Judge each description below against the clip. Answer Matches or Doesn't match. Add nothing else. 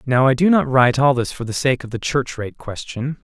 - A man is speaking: Matches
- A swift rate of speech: Matches